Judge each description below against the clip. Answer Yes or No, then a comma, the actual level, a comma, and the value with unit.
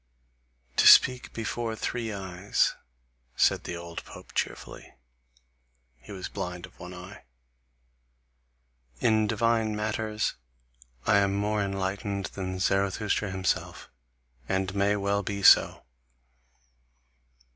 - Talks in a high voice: No, low, 100 Hz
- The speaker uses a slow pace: Yes, slow, 105 wpm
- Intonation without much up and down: Yes, narrow, 2.1 semitones